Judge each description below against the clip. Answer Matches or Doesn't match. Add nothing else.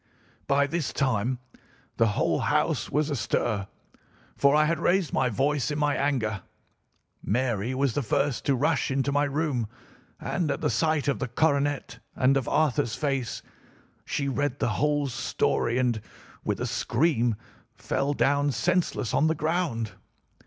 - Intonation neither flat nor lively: Matches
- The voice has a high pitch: Doesn't match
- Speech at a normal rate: Matches